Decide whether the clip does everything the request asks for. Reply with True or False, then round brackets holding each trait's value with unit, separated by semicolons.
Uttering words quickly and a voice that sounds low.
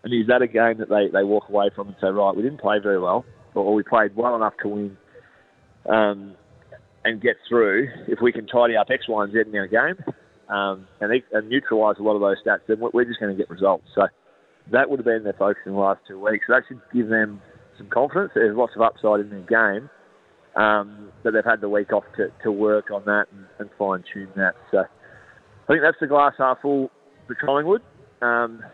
True (235 wpm; 105 Hz)